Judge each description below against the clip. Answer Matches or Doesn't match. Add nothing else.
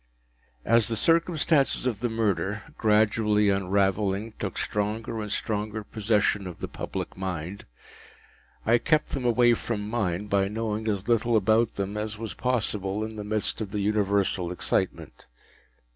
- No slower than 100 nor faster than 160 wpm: Matches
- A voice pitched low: Matches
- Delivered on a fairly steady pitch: Matches